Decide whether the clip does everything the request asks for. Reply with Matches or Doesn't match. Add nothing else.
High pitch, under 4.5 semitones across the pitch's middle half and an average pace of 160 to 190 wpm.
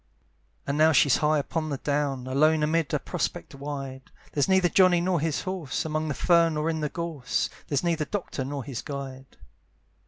Doesn't match